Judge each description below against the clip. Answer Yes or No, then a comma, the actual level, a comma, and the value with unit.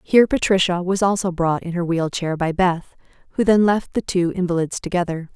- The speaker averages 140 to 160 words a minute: No, average, 200 wpm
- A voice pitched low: No, medium, 180 Hz